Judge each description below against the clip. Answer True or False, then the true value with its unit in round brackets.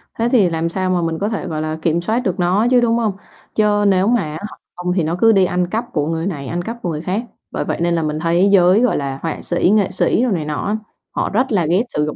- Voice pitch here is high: False (180 Hz)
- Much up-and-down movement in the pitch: False (4.4 semitones)